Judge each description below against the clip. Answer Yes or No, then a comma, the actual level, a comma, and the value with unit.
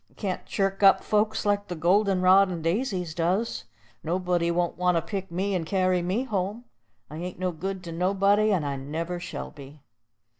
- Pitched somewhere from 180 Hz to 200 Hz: Yes, medium, 185 Hz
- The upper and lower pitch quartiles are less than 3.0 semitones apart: Yes, narrow, 2.6 semitones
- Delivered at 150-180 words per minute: No, average, 190 wpm